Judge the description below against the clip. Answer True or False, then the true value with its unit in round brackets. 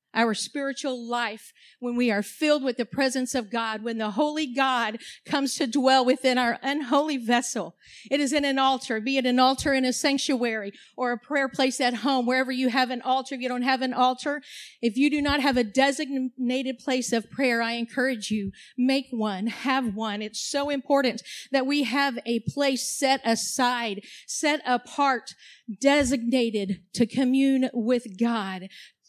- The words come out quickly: False (175 wpm)